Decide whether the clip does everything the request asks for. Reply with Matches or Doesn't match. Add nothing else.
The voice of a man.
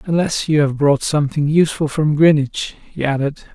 Matches